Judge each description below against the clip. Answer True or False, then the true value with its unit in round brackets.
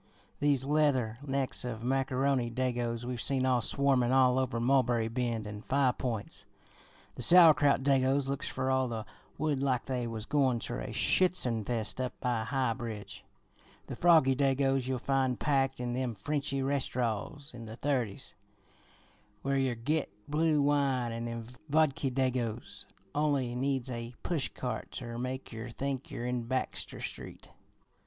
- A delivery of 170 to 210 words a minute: False (150 wpm)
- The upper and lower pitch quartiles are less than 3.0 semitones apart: True (2.6 semitones)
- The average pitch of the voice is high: False (130 Hz)